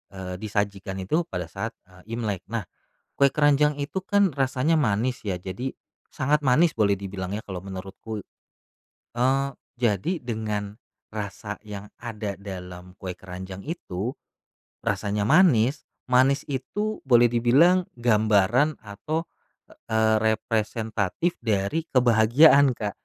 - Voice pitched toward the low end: Yes, low, 110 Hz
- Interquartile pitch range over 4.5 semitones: Yes, wide, 5.4 semitones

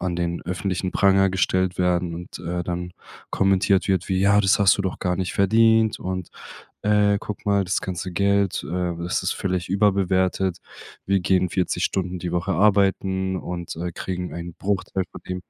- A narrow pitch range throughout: Yes, narrow, 1.7 semitones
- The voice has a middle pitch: No, very low, 95 Hz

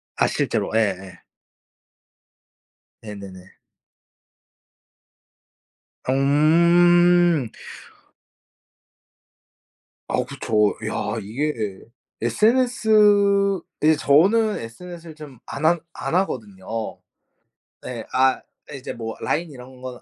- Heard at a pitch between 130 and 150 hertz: Yes, medium, 140 Hz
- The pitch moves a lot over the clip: Yes, wide, 7.6 semitones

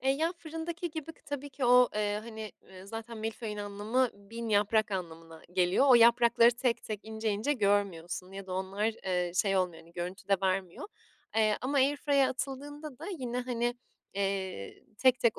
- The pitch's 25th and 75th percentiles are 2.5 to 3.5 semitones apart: No, average, 4.8 semitones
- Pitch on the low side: No, high, 220 Hz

